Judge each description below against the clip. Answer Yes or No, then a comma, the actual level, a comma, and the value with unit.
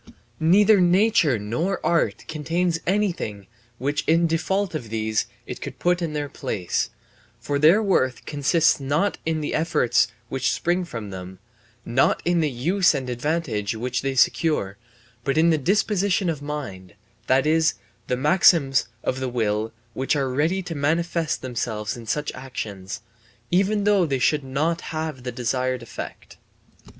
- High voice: No, medium, 150 Hz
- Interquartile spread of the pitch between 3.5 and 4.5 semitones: No, wide, 5.5 semitones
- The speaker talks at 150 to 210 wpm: Yes, average, 155 wpm